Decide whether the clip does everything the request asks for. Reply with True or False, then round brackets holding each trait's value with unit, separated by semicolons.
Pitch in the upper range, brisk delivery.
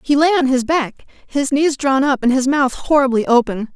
True (270 Hz; 225 wpm)